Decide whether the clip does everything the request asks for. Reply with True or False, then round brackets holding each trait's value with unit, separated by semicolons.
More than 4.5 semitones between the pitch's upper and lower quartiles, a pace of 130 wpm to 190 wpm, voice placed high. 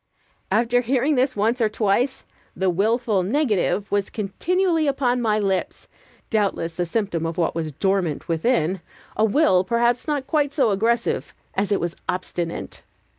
True (4.9 semitones; 155 wpm; 215 Hz)